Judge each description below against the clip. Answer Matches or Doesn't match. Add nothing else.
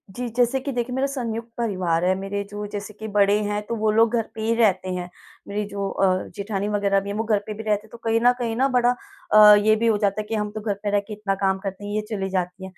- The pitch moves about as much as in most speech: Doesn't match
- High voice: Matches